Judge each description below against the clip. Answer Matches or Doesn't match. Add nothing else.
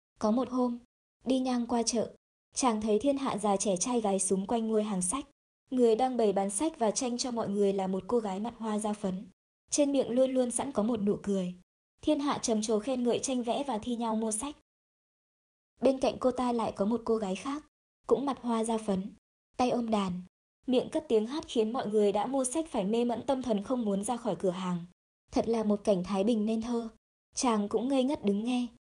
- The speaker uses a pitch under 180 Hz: Doesn't match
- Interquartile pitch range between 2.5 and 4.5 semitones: Matches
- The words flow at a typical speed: Matches